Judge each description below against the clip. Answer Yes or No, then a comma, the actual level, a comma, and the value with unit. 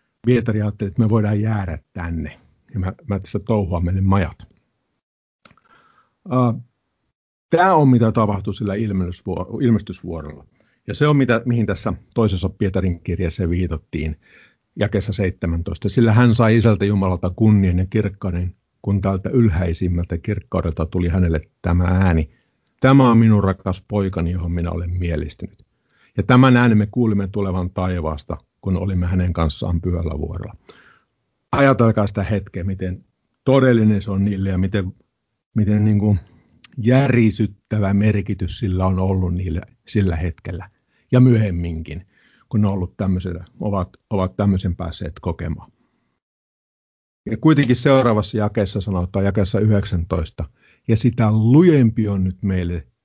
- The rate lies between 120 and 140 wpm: Yes, average, 130 wpm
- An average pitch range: Yes, average, 3.4 semitones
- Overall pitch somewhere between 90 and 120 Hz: Yes, low, 100 Hz